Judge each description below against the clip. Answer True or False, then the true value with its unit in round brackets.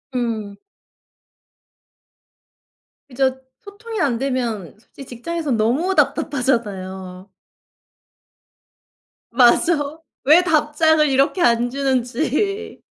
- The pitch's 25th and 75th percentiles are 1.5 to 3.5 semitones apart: False (5.3 semitones)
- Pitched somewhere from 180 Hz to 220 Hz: False (265 Hz)